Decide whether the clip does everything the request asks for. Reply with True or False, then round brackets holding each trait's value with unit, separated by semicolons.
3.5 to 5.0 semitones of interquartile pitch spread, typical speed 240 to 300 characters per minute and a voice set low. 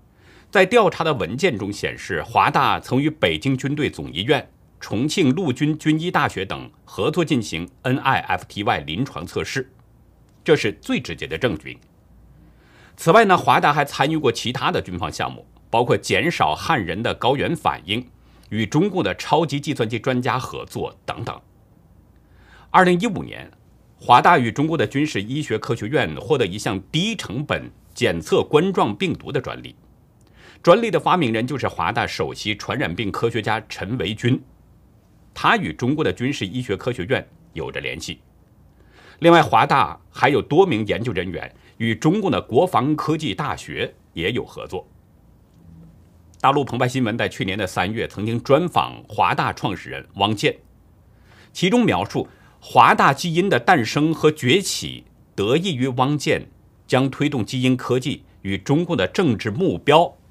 False (5.6 semitones; 245 characters per minute; 125 Hz)